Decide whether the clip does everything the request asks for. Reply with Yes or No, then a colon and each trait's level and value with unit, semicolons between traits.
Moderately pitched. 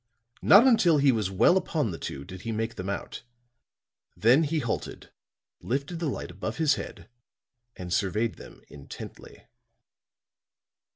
No: low, 115 Hz